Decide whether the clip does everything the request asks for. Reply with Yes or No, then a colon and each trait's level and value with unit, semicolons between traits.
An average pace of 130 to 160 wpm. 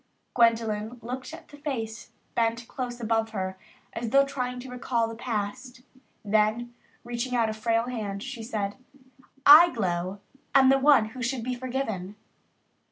Yes: average, 155 wpm